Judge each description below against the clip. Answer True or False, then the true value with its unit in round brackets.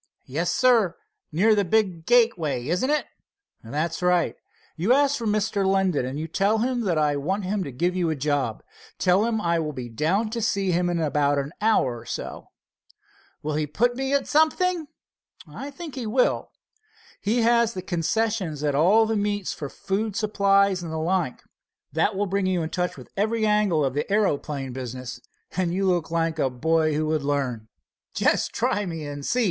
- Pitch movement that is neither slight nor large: False (6.0 semitones)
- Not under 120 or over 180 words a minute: False (190 wpm)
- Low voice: False (180 Hz)